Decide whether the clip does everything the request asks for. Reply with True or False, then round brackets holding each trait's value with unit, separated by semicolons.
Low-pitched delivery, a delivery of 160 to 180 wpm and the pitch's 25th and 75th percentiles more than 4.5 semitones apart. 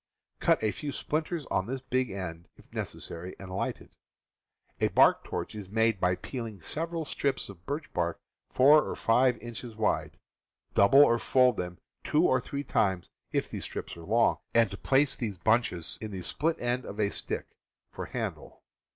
True (115 Hz; 175 wpm; 5.6 semitones)